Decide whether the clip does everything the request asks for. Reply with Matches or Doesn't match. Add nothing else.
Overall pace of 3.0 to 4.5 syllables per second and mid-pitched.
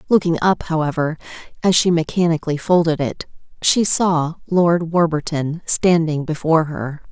Doesn't match